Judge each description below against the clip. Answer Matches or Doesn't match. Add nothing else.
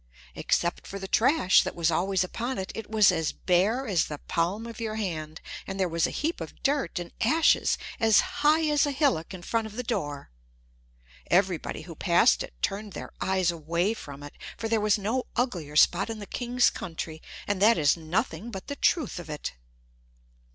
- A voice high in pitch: Matches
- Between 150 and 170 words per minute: Doesn't match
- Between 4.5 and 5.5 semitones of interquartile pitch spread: Matches